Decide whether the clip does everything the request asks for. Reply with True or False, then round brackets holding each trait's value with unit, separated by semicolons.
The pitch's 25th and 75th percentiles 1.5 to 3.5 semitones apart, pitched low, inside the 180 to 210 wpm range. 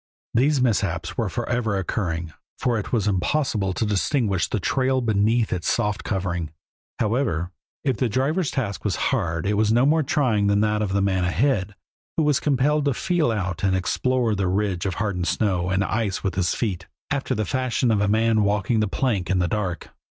False (4.7 semitones; 105 Hz; 195 wpm)